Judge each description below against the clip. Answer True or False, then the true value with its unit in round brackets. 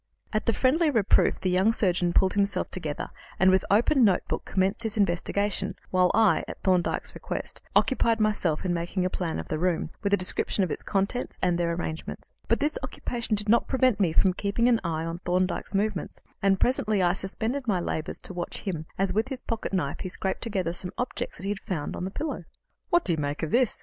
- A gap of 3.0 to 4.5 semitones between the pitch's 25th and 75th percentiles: True (3.8 semitones)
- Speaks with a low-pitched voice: False (195 Hz)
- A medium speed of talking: False (215 wpm)